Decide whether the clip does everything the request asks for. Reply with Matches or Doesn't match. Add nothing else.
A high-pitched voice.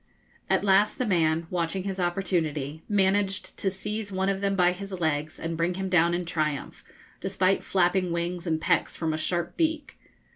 Doesn't match